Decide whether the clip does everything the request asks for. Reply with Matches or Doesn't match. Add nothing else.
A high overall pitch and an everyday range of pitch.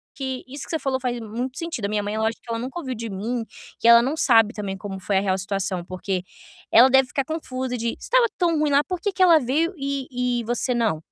Matches